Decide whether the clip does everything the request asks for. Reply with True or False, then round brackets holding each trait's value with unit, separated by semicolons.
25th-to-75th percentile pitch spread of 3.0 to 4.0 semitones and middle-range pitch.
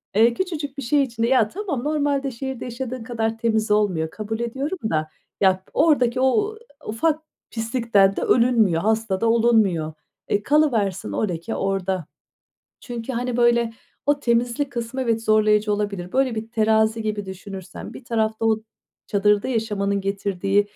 False (3.5 semitones; 225 Hz)